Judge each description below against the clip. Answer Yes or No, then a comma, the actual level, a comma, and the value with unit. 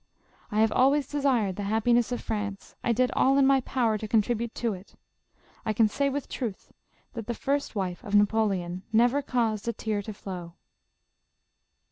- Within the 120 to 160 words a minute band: No, average, 180 wpm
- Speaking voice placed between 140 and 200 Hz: No, high, 225 Hz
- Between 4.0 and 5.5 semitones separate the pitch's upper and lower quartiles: No, average, 3.4 semitones